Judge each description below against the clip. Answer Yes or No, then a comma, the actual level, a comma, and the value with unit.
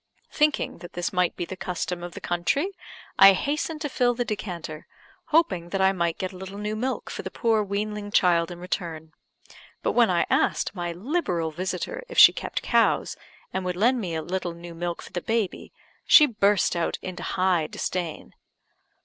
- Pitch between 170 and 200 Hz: Yes, medium, 185 Hz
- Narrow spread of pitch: No, average, 3.9 semitones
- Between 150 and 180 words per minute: No, average, 190 wpm